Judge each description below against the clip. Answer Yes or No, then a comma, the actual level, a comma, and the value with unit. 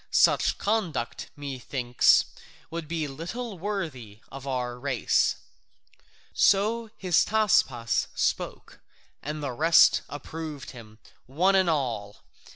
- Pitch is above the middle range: No, medium, 150 Hz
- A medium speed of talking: No, slow, 100 wpm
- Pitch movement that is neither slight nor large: No, wide, 6.6 semitones